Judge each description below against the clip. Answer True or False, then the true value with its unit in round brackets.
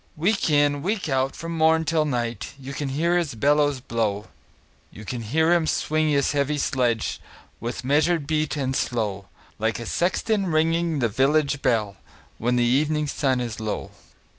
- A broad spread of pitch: False (4.5 semitones)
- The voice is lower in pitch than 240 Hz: True (140 Hz)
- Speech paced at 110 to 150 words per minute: False (165 wpm)